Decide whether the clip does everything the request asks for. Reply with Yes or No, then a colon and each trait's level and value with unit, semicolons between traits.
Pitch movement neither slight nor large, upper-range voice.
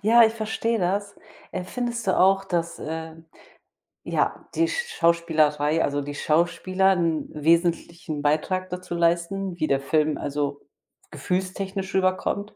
No: average, 3.5 semitones; medium, 175 Hz